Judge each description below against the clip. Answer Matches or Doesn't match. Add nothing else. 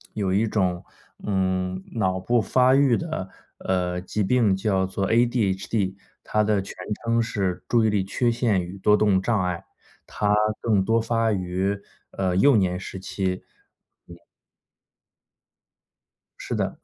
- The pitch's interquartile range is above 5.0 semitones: Doesn't match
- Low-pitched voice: Matches